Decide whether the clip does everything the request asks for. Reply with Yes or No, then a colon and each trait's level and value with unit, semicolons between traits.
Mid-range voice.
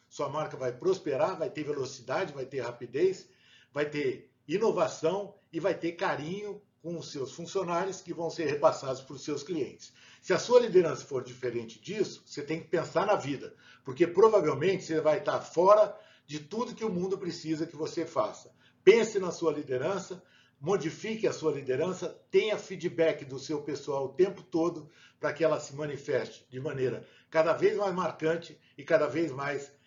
Yes: medium, 160 Hz